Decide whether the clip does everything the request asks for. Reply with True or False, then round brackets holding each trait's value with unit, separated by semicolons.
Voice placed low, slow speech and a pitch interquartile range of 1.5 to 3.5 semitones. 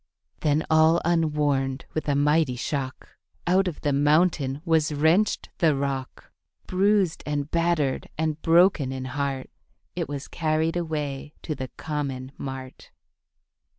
False (150 Hz; 130 wpm; 3.0 semitones)